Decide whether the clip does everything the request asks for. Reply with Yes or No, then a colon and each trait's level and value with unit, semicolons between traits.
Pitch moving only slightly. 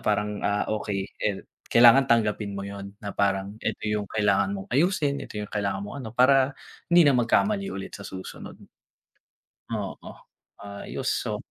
No: average, 3.7 semitones